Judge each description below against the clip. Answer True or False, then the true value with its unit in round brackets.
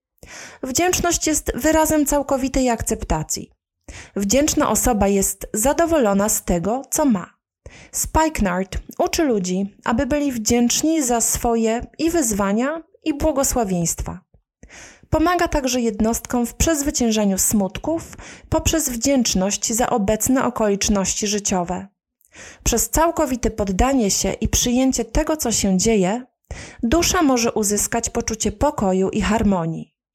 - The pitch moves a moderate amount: False (6.1 semitones)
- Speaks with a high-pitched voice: True (235 Hz)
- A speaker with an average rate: False (105 wpm)